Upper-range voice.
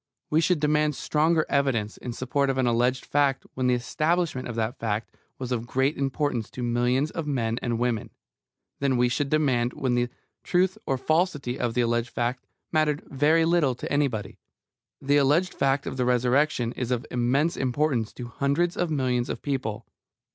No: low, 130 Hz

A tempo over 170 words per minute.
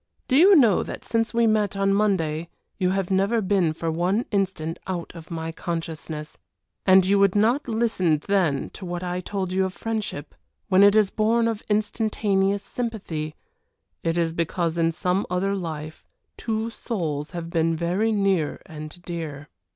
No: average, 165 wpm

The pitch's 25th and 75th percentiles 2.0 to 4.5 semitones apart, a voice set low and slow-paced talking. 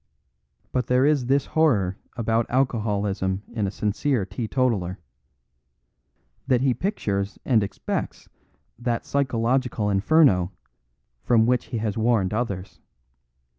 Yes: average, 4.2 semitones; low, 115 Hz; slow, 110 wpm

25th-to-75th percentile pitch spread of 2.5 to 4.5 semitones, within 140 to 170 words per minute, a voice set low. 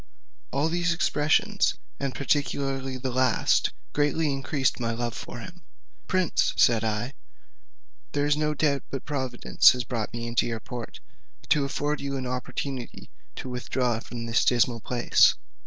Yes: average, 3.2 semitones; average, 150 wpm; low, 130 Hz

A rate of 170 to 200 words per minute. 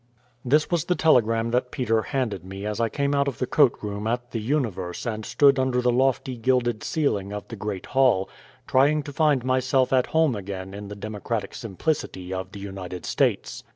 Yes: average, 195 wpm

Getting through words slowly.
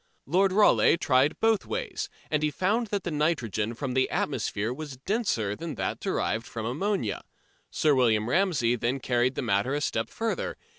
No: average, 170 wpm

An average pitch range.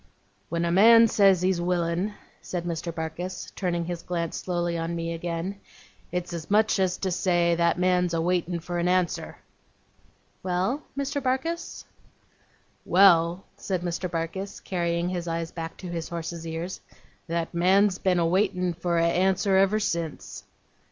No: narrow, 1.9 semitones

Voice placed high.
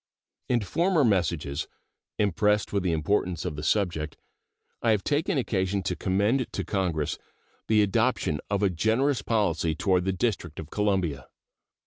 No: low, 100 Hz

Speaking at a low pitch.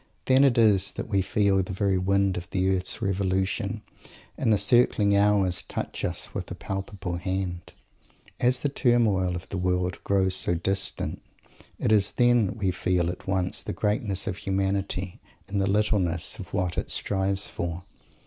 Yes: very low, 95 Hz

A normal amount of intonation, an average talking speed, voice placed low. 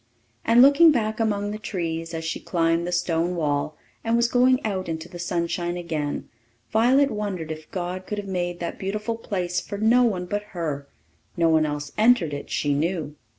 No: average, 4.6 semitones; average, 190 wpm; medium, 180 Hz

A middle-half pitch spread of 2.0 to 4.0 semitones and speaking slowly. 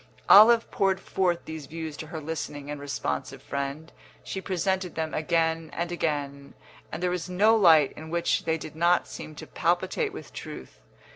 No: average, 2.7 semitones; average, 170 wpm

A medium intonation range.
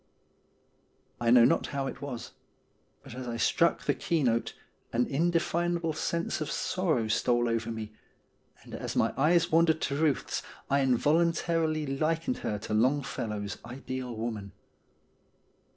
No: wide, 5.7 semitones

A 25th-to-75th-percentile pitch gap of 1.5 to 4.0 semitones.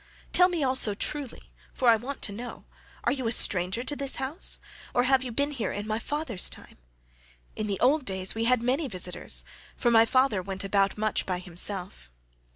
No: average, 5.2 semitones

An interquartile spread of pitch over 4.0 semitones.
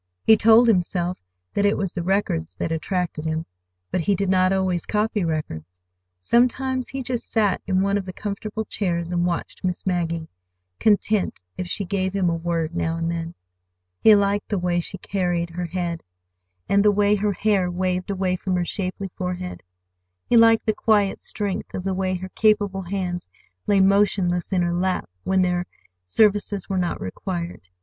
No: narrow, 2.6 semitones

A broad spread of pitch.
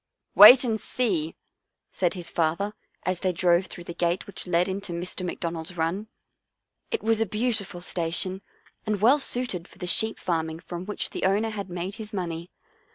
No: average, 3.6 semitones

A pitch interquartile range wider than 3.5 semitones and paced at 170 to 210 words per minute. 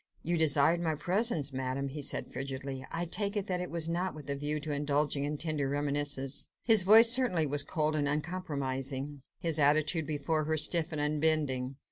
No: average, 3.0 semitones; average, 185 wpm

